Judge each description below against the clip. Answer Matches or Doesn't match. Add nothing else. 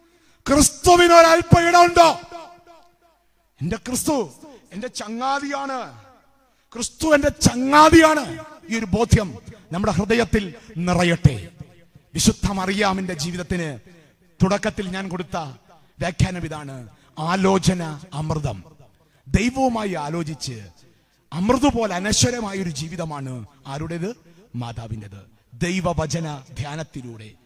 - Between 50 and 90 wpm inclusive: Matches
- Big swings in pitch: Matches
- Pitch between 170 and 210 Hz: Matches